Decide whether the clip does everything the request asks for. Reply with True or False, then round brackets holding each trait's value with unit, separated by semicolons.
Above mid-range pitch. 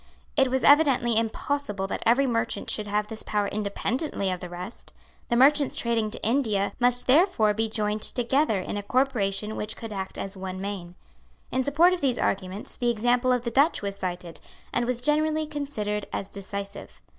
True (225 Hz)